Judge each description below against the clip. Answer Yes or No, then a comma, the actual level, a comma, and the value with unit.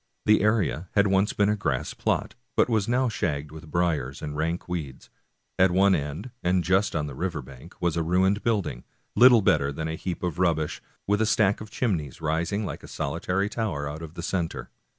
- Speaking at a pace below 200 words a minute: No, fast, 205 wpm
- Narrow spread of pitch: No, average, 4.6 semitones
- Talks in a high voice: No, very low, 90 Hz